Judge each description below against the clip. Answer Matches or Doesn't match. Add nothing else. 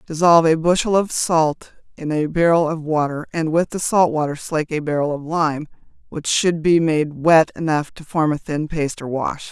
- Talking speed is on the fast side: Matches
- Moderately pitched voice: Matches